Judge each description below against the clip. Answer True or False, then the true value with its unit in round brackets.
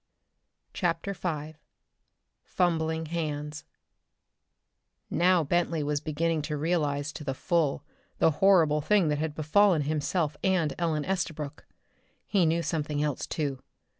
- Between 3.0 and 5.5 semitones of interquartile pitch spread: False (2.4 semitones)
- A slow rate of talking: True (120 wpm)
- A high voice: False (155 Hz)